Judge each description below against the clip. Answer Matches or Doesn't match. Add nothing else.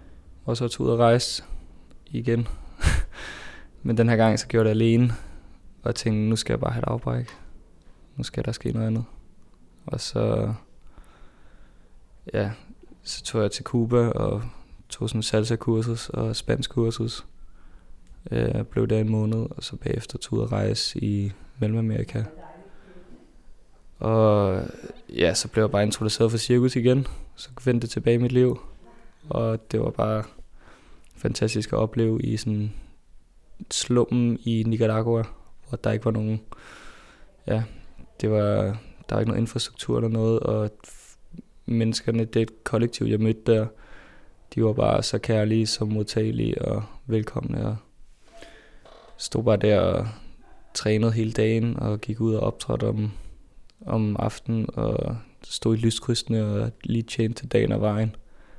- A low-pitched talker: Matches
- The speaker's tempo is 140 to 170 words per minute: Matches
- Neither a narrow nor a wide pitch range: Doesn't match